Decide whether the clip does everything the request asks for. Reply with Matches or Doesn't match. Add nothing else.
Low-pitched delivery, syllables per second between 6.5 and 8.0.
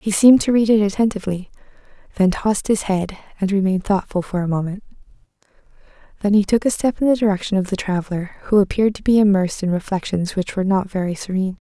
Doesn't match